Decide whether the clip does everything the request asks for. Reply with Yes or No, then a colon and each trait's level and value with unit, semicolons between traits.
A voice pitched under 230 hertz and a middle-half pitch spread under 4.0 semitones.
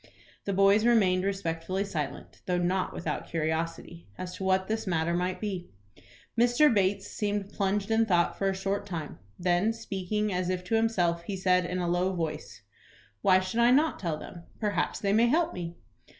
Yes: high, 190 Hz; average, 2.9 semitones